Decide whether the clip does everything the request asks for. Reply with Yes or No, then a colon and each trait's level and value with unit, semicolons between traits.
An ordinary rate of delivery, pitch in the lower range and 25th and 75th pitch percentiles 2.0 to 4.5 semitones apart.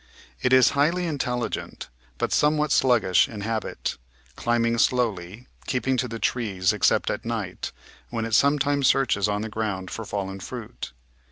Yes: average, 155 wpm; low, 115 Hz; average, 3.9 semitones